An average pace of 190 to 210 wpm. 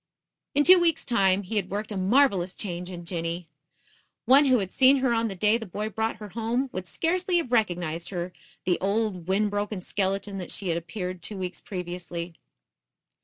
Yes: average, 195 wpm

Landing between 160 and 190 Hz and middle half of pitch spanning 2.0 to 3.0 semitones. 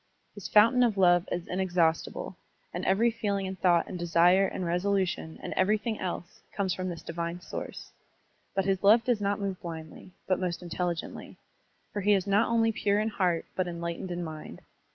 Yes: medium, 185 Hz; average, 2.7 semitones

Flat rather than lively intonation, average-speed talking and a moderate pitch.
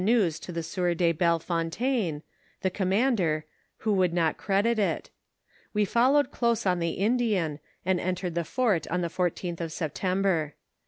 No: average, 3.8 semitones; average, 160 wpm; medium, 180 Hz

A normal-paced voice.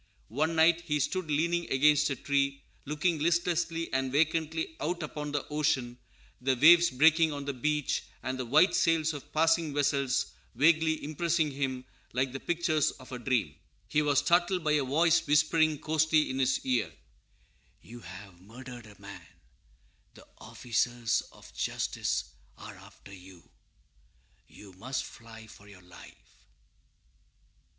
Yes: average, 145 wpm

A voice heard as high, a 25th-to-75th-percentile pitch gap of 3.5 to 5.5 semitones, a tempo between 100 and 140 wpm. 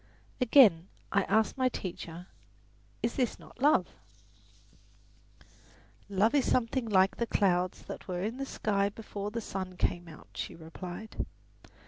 Yes: high, 200 Hz; average, 4.2 semitones; slow, 135 wpm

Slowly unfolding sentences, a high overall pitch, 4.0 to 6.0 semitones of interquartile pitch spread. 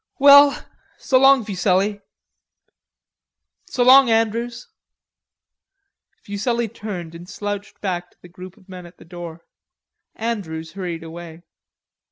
Yes: slow, 115 wpm; high, 200 Hz; average, 5.1 semitones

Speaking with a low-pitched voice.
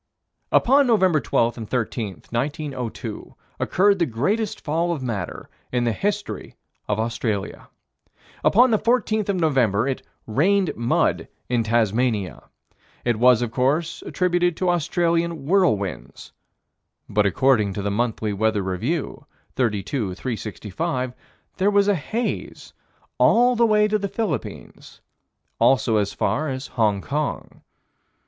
Yes: low, 130 Hz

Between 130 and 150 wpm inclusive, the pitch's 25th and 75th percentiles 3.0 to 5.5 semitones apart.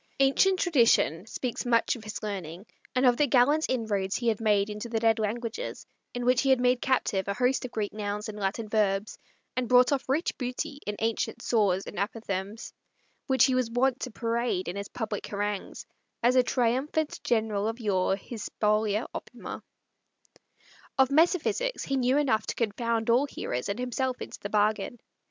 No: average, 180 wpm; average, 3.5 semitones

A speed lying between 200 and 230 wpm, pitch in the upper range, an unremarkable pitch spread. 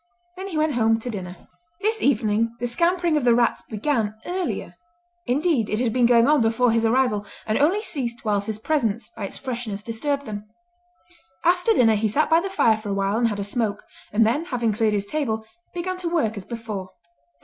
No: fast, 205 wpm; high, 235 Hz; wide, 5.7 semitones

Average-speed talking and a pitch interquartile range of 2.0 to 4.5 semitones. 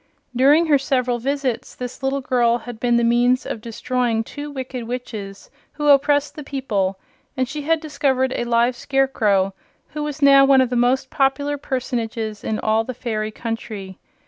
Yes: average, 170 wpm; average, 3.1 semitones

